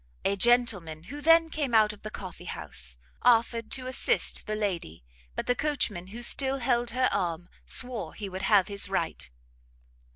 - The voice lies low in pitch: No, high, 215 Hz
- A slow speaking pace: No, average, 170 wpm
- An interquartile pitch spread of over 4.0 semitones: Yes, average, 5.2 semitones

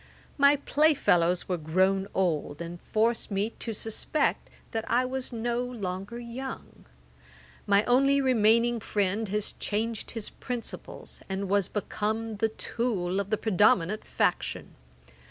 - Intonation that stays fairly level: No, average, 3.6 semitones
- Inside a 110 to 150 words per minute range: Yes, slow, 135 wpm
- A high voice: Yes, high, 215 Hz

